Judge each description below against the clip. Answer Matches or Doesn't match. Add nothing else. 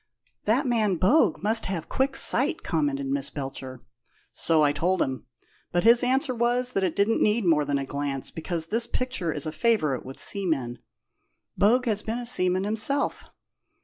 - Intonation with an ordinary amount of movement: Doesn't match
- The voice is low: Doesn't match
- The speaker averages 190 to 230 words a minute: Doesn't match